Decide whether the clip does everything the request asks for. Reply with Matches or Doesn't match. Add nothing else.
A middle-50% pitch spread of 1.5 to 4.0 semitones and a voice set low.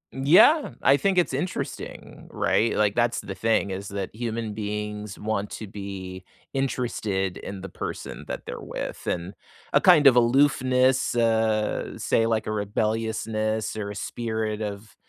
Matches